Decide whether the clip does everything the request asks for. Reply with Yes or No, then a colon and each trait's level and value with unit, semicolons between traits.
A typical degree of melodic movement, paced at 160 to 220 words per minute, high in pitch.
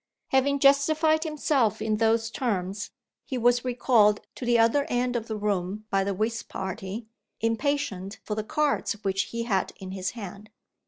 Yes: average, 4.1 semitones; average, 165 wpm; high, 225 Hz